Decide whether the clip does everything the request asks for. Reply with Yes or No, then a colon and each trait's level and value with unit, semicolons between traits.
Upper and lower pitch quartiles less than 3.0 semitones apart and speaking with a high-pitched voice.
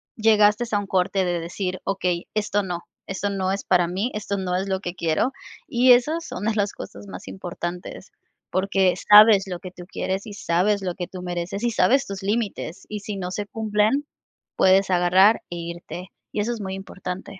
Yes: narrow, 2.6 semitones; high, 195 Hz